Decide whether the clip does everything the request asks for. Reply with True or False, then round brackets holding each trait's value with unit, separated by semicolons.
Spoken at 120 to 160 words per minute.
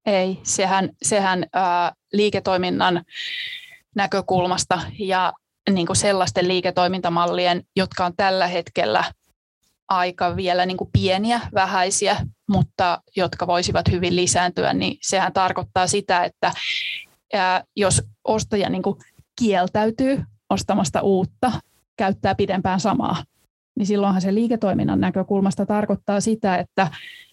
False (105 wpm)